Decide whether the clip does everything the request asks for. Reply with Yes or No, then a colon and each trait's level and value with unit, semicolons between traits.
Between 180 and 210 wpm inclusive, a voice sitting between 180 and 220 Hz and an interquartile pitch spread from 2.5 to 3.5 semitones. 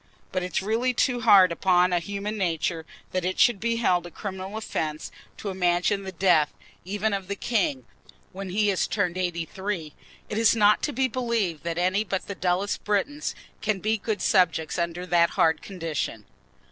Yes: average, 185 wpm; high, 190 Hz; average, 3.2 semitones